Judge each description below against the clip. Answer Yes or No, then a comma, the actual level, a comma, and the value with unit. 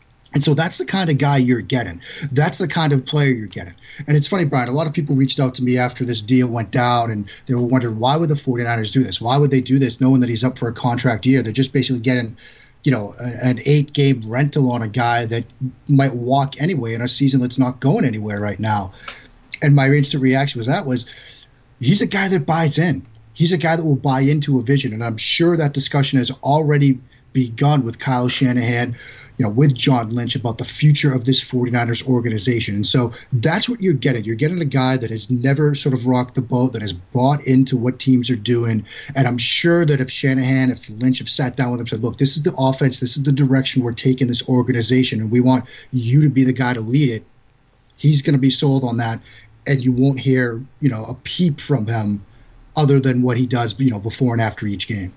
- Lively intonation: No, average, 2.7 semitones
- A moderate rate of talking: No, fast, 240 wpm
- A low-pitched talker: Yes, low, 130 Hz